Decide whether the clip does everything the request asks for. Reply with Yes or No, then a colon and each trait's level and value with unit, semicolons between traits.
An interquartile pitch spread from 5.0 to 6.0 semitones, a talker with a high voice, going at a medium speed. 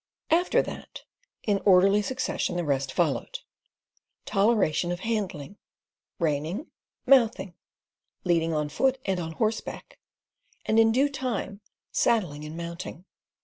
No: wide, 5.5 semitones; high, 195 Hz; slow, 115 wpm